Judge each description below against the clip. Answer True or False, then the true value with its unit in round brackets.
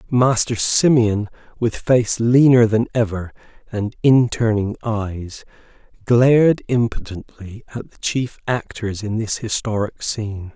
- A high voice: False (115 Hz)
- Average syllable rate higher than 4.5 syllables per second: False (3.9 syllables/s)